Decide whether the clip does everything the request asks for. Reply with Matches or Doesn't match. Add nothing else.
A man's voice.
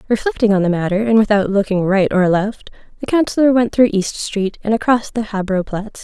Doesn't match